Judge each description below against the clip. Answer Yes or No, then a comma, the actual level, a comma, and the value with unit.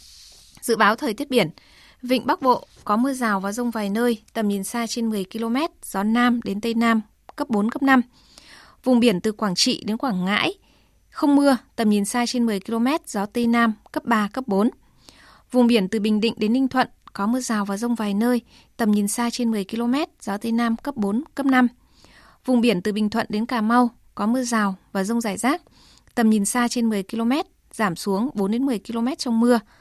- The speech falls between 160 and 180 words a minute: No, average, 215 wpm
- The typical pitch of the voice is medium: No, high, 230 Hz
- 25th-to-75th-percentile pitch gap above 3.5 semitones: No, average, 2.7 semitones